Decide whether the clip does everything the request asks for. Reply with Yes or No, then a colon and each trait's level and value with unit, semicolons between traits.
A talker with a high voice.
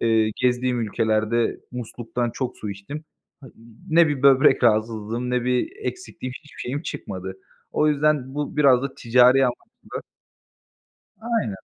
No: low, 125 Hz